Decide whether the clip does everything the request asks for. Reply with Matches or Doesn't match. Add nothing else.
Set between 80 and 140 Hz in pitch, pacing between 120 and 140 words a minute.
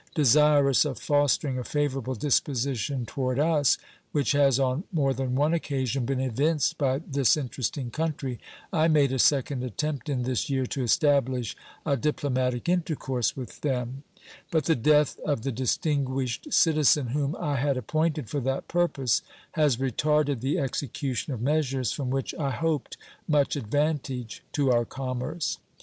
Doesn't match